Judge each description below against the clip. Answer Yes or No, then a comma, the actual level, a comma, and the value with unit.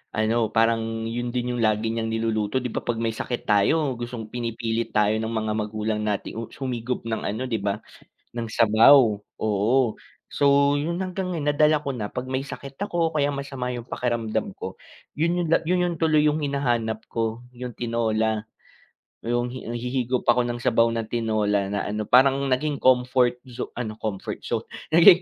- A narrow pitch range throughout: No, average, 3.3 semitones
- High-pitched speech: No, low, 120 Hz